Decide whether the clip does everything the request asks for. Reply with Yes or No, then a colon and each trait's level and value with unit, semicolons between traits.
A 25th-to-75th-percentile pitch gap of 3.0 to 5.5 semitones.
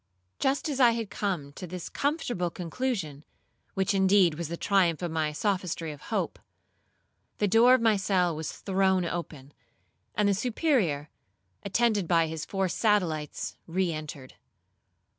Yes: average, 4.4 semitones